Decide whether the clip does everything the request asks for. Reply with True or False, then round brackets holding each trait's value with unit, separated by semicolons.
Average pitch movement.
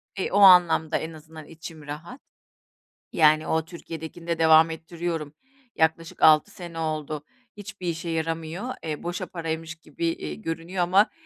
False (1.6 semitones)